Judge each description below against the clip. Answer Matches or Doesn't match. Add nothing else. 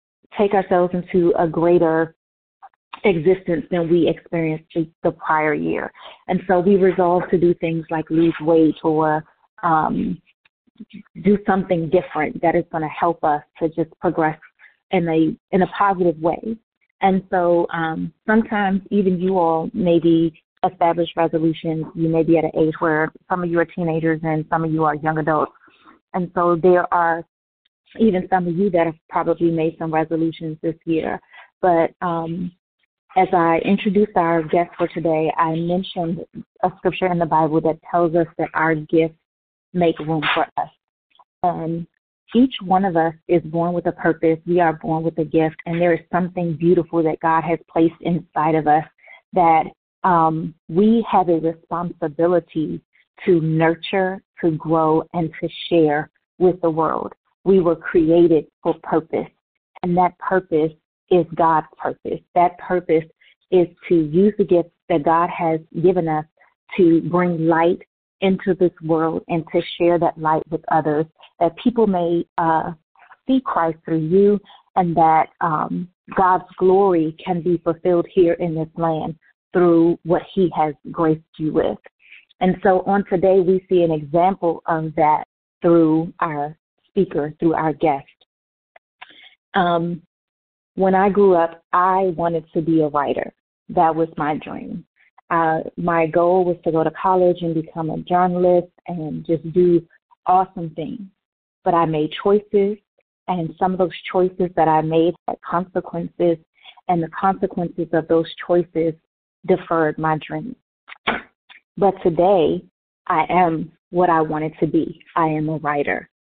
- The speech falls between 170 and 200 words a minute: Doesn't match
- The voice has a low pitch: Doesn't match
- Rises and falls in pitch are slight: Matches